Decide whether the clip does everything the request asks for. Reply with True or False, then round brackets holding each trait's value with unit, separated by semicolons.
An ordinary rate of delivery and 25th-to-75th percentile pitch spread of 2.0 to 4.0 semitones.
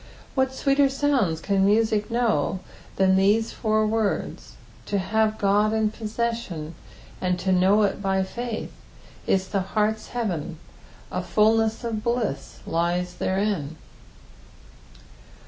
False (125 wpm; 3.0 semitones)